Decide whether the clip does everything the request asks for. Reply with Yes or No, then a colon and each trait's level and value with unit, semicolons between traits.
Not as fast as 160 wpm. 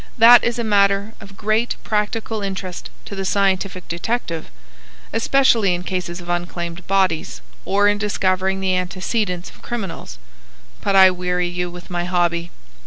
Yes: average, 145 wpm